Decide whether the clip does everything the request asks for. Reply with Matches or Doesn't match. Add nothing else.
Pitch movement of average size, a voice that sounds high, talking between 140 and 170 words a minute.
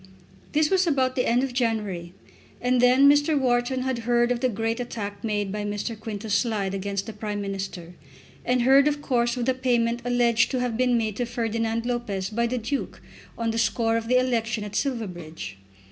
Doesn't match